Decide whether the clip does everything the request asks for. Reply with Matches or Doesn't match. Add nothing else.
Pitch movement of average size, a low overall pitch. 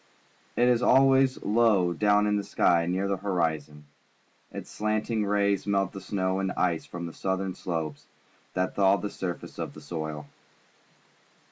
Matches